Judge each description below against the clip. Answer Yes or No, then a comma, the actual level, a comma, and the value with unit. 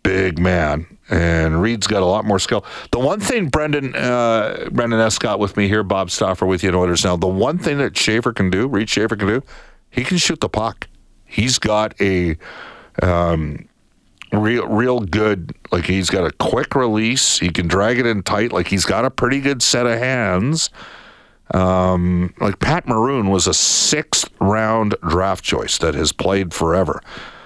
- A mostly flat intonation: No, average, 4.2 semitones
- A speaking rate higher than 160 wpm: Yes, average, 185 wpm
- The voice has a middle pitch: No, low, 105 Hz